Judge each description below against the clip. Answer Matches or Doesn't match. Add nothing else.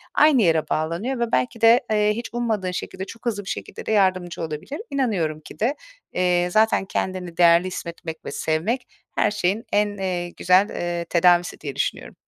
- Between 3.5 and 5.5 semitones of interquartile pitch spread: Matches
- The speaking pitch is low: Doesn't match